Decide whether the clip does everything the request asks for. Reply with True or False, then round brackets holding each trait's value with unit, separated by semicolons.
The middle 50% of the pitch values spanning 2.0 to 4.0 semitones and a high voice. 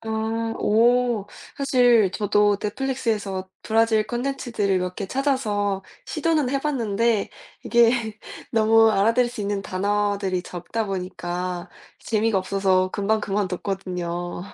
True (3.1 semitones; 210 Hz)